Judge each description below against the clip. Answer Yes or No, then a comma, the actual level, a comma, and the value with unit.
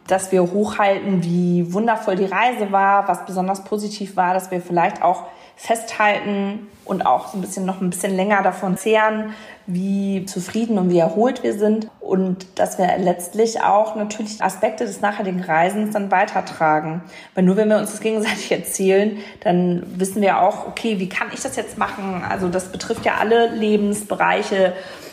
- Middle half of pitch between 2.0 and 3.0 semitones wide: Yes, narrow, 2.5 semitones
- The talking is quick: No, average, 170 wpm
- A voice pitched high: Yes, high, 195 Hz